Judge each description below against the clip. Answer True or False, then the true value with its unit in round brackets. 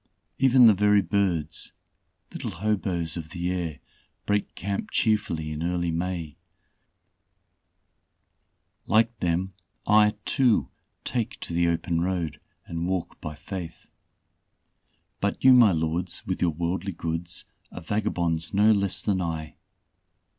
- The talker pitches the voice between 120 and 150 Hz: False (90 Hz)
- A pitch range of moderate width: True (3.7 semitones)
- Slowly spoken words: True (125 wpm)